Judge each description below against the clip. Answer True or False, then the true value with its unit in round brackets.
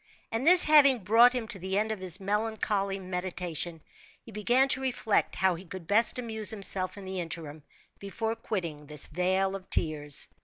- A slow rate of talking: False (180 wpm)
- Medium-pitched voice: False (195 Hz)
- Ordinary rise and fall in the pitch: True (3.9 semitones)